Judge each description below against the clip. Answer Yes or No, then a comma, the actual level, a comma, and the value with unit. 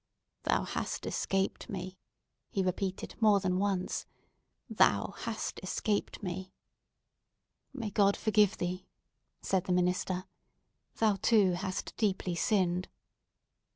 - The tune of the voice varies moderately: No, narrow, 2.0 semitones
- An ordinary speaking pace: No, slow, 110 wpm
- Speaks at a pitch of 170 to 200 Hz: Yes, high, 190 Hz